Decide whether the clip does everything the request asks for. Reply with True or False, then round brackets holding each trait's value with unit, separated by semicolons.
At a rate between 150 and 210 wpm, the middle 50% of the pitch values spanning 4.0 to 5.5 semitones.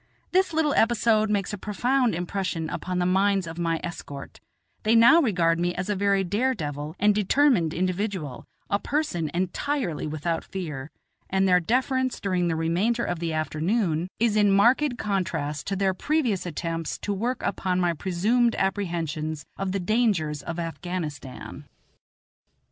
True (155 wpm; 4.6 semitones)